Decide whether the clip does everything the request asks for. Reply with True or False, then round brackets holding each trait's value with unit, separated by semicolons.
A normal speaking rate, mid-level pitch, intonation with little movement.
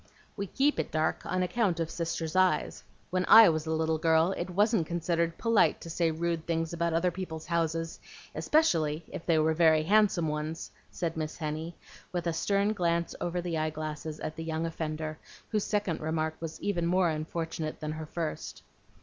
True (185 wpm; 165 Hz; 1.9 semitones)